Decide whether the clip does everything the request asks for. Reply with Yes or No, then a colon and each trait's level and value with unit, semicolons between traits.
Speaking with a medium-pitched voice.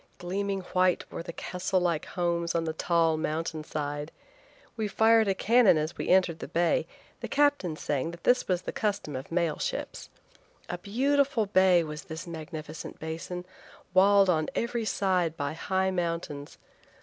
Yes: medium, 175 Hz